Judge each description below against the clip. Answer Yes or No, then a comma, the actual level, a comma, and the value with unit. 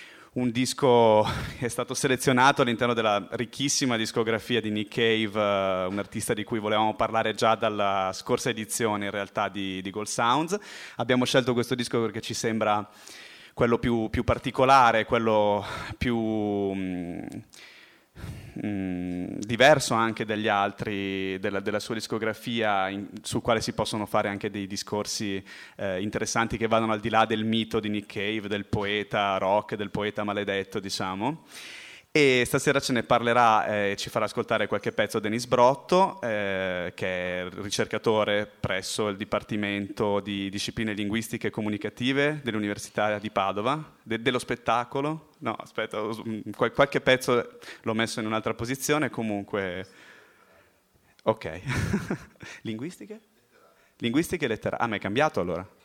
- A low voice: Yes, low, 110 Hz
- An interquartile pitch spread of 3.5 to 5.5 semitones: No, average, 2.8 semitones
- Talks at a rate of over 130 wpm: Yes, average, 140 wpm